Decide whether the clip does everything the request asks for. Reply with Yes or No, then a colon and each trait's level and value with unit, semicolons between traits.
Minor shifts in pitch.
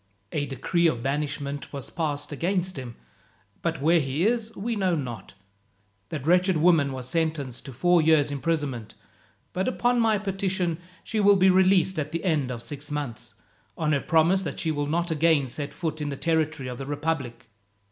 No: average, 4.1 semitones